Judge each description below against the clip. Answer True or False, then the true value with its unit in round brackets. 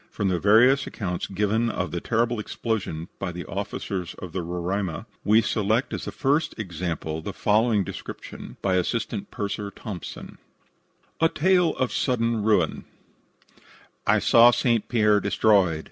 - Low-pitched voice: True (105 Hz)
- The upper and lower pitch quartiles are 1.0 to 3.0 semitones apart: False (3.9 semitones)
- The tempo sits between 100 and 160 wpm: True (140 wpm)